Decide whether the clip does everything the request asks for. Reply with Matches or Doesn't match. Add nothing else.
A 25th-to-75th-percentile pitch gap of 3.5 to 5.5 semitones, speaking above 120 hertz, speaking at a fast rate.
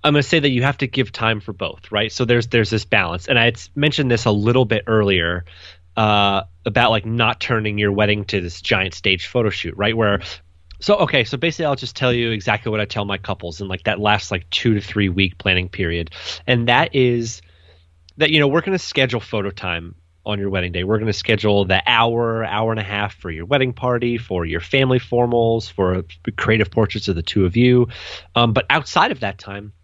Doesn't match